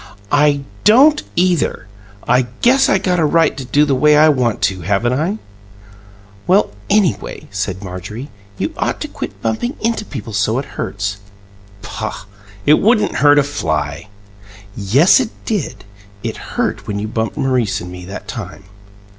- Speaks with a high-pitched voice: No, low, 135 Hz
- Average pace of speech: Yes, average, 160 wpm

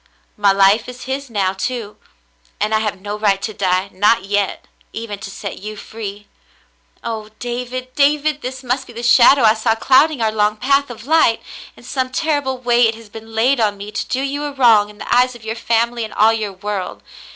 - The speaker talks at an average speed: No, fast, 210 wpm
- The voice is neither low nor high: No, high, 225 Hz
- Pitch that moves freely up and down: No, average, 3.4 semitones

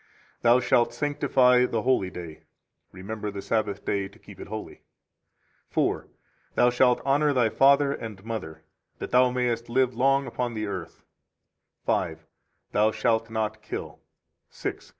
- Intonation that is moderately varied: Yes, average, 3.4 semitones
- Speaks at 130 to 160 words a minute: Yes, average, 155 wpm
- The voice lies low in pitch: Yes, low, 115 Hz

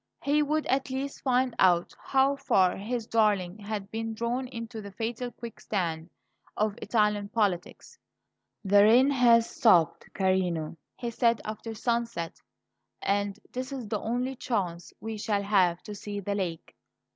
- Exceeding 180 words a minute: No, average, 145 wpm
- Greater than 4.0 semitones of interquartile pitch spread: No, average, 3.5 semitones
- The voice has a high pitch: Yes, high, 220 Hz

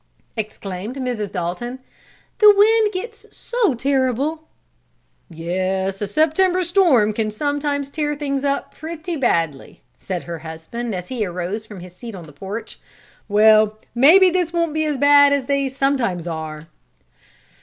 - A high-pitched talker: Yes, very high, 250 Hz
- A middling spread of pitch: No, wide, 8.0 semitones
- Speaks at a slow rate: No, average, 145 wpm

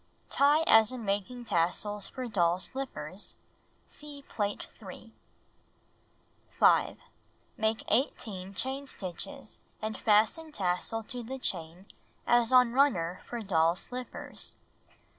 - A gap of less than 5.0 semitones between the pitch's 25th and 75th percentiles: No, wide, 5.4 semitones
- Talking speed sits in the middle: No, slow, 110 wpm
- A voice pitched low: No, high, 220 Hz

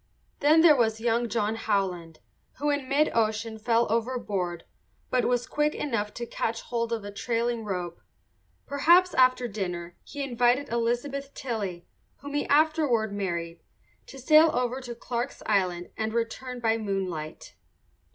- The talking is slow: No, average, 145 wpm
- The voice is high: Yes, high, 230 Hz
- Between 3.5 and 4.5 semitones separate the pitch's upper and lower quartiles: Yes, average, 4.1 semitones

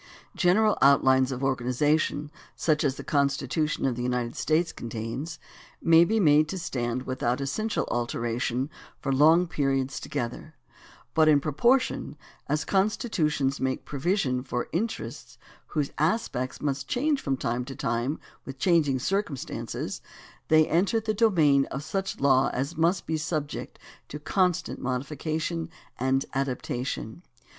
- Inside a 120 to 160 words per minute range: Yes, slow, 135 wpm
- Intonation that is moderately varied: Yes, average, 4.1 semitones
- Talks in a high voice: No, medium, 145 Hz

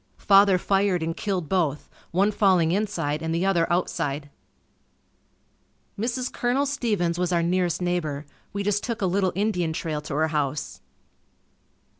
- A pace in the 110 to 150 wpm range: Yes, average, 145 wpm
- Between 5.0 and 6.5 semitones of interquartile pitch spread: No, average, 3.7 semitones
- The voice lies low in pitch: No, medium, 180 Hz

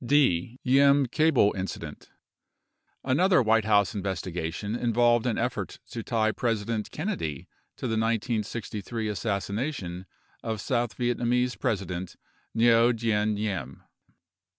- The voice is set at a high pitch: No, low, 115 Hz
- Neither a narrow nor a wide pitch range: Yes, average, 3.2 semitones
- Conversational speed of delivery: No, slow, 115 wpm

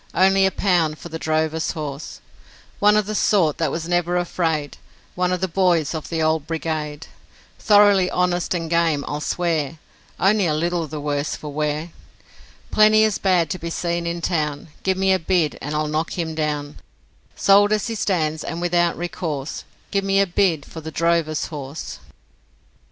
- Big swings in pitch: No, average, 3.1 semitones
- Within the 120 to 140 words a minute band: No, average, 180 wpm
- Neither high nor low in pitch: Yes, medium, 165 Hz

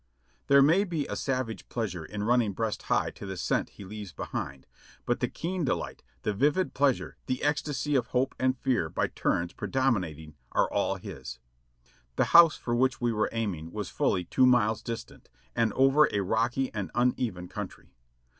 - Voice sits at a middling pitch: No, low, 120 Hz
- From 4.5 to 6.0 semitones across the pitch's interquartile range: Yes, average, 4.8 semitones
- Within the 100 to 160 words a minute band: No, average, 180 wpm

